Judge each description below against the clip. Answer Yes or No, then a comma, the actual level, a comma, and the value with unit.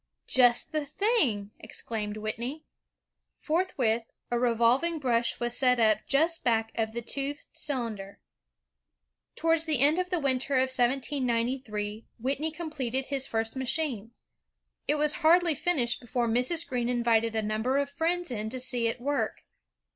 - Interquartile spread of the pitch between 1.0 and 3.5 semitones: No, average, 4.5 semitones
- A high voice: Yes, very high, 255 Hz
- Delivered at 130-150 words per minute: Yes, average, 145 wpm